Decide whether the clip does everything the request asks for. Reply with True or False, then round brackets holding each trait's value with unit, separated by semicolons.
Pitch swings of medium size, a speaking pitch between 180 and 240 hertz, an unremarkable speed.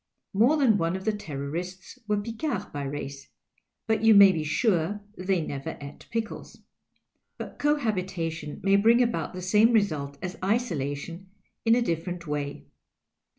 False (5.9 semitones; 185 Hz; 150 wpm)